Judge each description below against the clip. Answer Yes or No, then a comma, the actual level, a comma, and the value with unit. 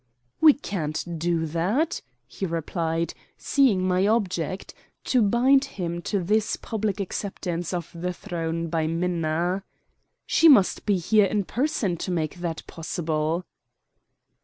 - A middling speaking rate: No, slow, 130 wpm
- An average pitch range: Yes, average, 3.8 semitones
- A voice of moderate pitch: Yes, medium, 180 Hz